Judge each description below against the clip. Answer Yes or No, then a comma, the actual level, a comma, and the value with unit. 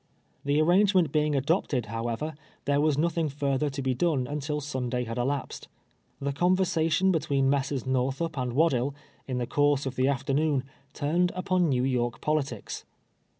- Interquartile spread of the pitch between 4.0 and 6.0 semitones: No, average, 3.2 semitones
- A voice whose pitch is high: No, medium, 140 Hz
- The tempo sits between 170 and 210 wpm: No, average, 150 wpm